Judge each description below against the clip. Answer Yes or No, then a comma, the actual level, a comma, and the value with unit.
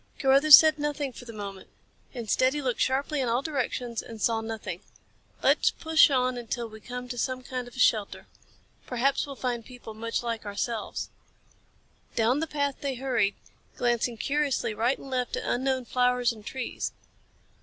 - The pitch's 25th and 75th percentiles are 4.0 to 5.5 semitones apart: No, average, 2.8 semitones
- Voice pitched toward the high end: Yes, very high, 250 Hz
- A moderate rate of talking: Yes, average, 170 wpm